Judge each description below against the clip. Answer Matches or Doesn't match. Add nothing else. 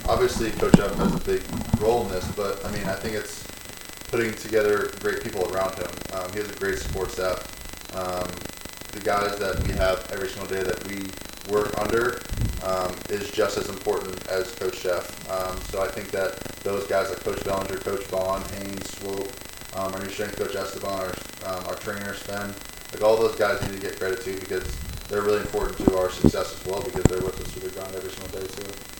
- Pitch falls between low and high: Doesn't match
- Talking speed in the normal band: Doesn't match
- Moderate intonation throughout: Doesn't match